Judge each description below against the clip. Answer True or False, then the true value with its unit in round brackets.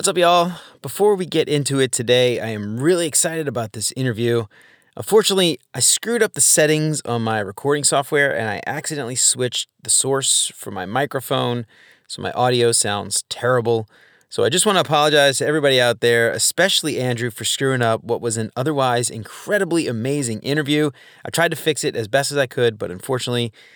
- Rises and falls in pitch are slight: False (4.6 semitones)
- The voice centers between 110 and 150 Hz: True (135 Hz)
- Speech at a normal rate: True (185 wpm)